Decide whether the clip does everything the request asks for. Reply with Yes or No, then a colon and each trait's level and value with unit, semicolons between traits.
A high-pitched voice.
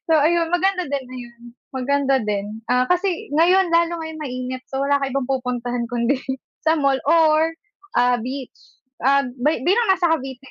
Yes: very high, 275 Hz